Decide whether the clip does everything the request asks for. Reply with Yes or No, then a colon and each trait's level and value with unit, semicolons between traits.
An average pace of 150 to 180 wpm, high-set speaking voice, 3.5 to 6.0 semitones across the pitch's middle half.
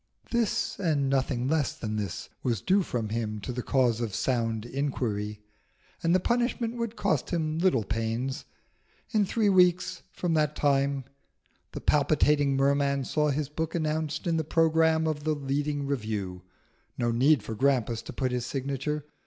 No: average, 160 wpm; medium, 140 Hz; average, 4.7 semitones